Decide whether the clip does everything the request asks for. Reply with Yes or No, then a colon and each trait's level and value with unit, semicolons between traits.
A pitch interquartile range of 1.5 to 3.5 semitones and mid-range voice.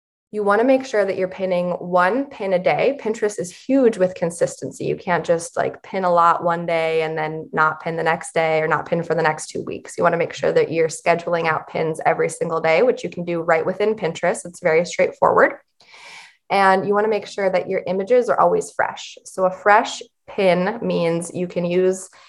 No: average, 4.0 semitones; medium, 180 Hz